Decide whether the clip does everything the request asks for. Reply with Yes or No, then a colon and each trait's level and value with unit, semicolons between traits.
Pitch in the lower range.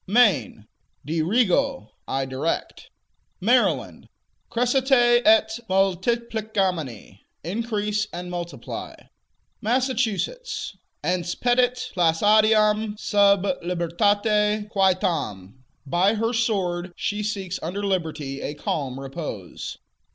No: high, 200 Hz